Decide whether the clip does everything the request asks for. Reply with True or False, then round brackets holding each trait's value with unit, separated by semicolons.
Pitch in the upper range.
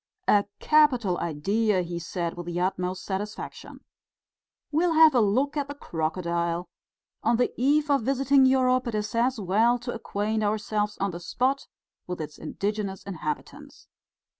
True (215 Hz)